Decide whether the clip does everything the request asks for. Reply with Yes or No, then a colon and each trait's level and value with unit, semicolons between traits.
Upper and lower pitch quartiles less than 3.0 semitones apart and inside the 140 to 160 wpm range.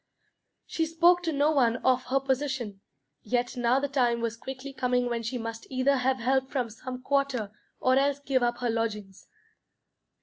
No: narrow, 2.6 semitones; average, 175 wpm